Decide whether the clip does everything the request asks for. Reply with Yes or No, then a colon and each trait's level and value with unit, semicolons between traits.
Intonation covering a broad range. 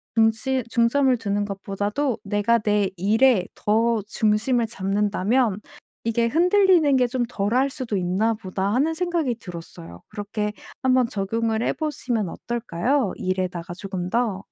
No: average, 4.2 semitones